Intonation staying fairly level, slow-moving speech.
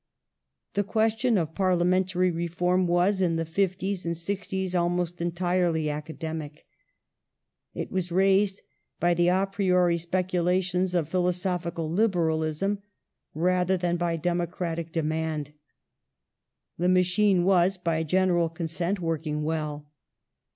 Yes: narrow, 2.1 semitones; slow, 110 wpm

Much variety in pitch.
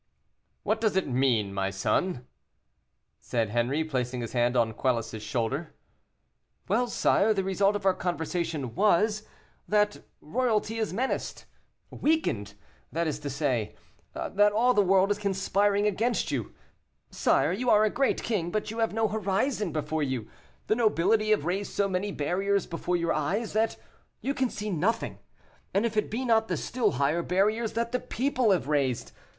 Yes: wide, 6.9 semitones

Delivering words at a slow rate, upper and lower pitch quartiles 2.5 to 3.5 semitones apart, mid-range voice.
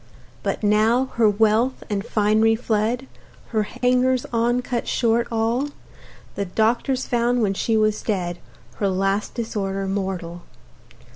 No: slow, 130 wpm; average, 2.9 semitones; high, 220 Hz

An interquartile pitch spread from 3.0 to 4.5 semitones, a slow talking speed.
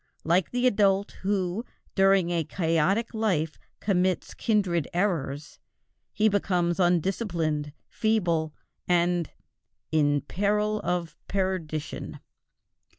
Yes: average, 3.6 semitones; slow, 90 wpm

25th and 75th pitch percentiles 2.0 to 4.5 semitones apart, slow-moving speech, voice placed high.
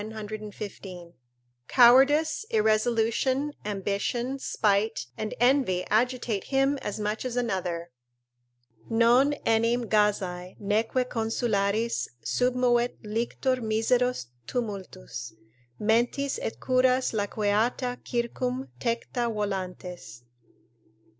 Yes: average, 3.4 semitones; slow, 80 wpm; high, 230 Hz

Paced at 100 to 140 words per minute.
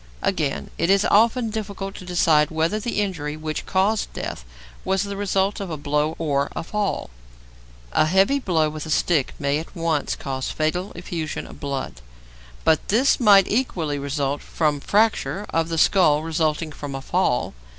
No: average, 170 wpm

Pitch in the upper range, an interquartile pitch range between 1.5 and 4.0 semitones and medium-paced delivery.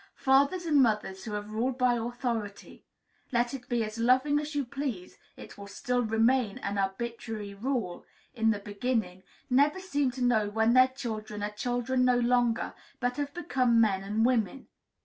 Yes: high, 240 Hz; average, 3.4 semitones; average, 170 wpm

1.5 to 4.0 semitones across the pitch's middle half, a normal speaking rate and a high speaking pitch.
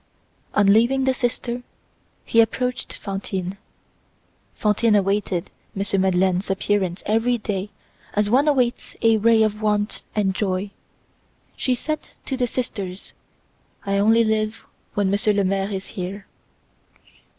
No: average, 2.9 semitones; slow, 130 wpm; high, 210 Hz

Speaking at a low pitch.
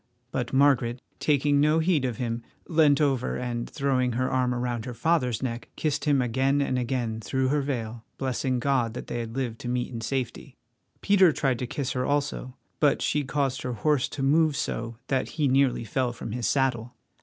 Yes: low, 130 Hz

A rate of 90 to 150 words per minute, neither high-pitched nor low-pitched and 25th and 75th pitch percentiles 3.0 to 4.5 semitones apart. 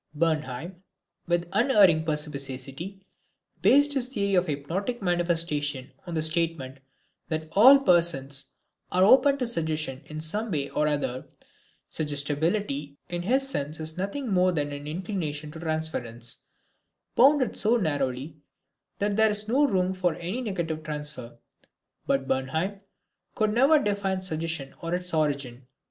No: slow, 135 wpm; medium, 165 Hz; average, 5.3 semitones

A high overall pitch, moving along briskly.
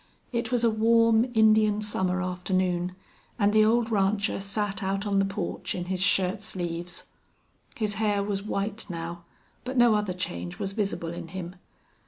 No: high, 200 Hz; average, 165 wpm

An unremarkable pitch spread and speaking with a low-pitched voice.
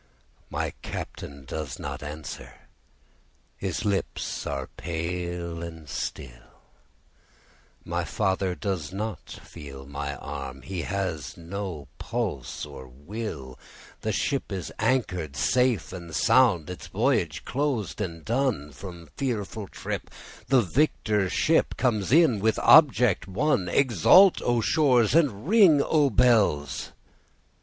No: wide, 7.5 semitones; very low, 95 Hz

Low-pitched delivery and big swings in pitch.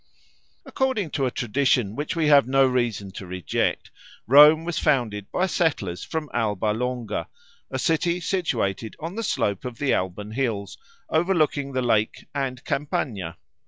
Yes: low, 130 Hz; wide, 6.5 semitones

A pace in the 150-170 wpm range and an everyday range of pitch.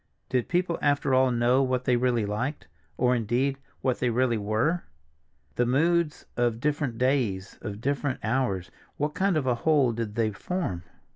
Yes: average, 160 wpm; average, 3.8 semitones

